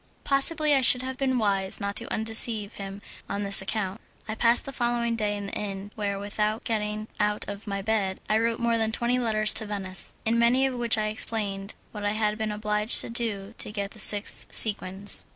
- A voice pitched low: No, high, 215 Hz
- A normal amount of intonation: No, narrow, 2.3 semitones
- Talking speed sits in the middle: No, fast, 210 wpm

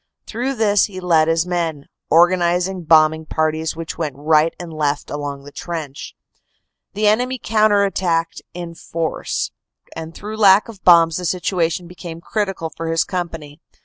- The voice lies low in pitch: No, medium, 170 Hz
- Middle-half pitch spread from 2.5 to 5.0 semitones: Yes, average, 3.0 semitones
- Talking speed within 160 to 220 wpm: No, average, 150 wpm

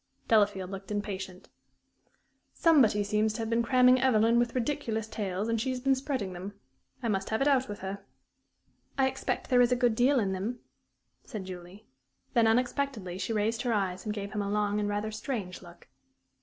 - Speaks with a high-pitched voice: Yes, high, 215 Hz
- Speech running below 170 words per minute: No, average, 185 wpm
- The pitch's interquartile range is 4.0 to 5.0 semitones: No, average, 3.6 semitones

